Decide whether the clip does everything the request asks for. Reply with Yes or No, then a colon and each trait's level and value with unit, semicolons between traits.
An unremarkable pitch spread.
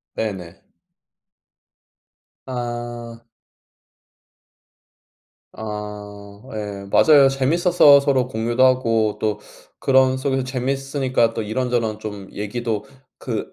Yes: average, 3.8 semitones